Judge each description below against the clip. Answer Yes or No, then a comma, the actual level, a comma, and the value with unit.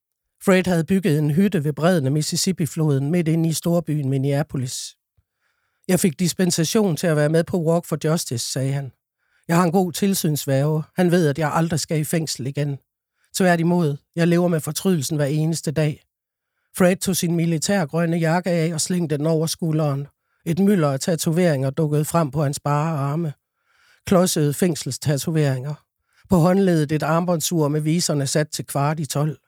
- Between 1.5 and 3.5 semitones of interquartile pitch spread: Yes, average, 3.0 semitones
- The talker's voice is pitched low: No, medium, 160 Hz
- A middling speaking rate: Yes, average, 170 wpm